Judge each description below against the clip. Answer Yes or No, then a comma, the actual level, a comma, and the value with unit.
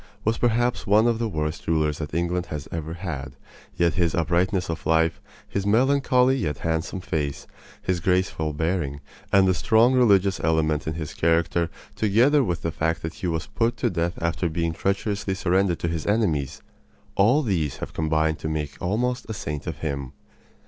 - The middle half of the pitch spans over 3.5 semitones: Yes, average, 4.4 semitones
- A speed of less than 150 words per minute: No, average, 175 wpm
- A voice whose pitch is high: No, very low, 85 Hz